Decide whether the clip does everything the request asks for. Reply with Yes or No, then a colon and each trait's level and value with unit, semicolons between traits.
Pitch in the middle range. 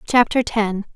No: high, 215 Hz